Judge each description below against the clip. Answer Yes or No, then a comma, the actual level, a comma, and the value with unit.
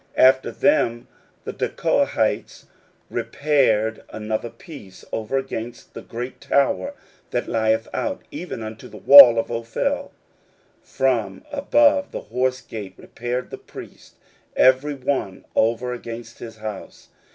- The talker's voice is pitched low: Yes, low, 120 Hz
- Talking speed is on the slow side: Yes, slow, 130 wpm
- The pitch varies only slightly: No, average, 3.5 semitones